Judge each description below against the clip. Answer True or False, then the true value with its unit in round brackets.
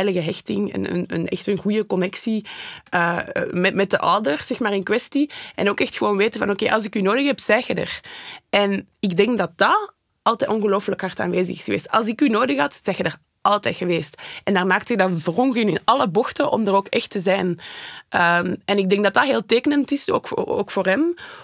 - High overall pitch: True (200 Hz)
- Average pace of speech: False (230 wpm)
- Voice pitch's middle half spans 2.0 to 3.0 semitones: False (3.7 semitones)